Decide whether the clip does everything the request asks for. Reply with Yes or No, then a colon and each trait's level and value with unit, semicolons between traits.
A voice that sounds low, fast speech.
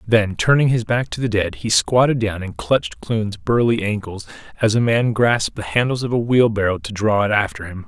Yes: low, 110 Hz; fast, 220 wpm